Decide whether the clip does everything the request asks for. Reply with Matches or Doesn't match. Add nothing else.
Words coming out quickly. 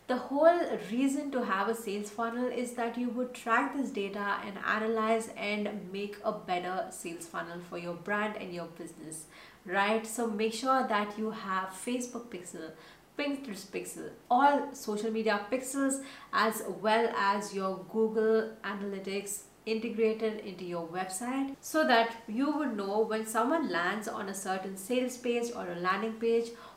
Doesn't match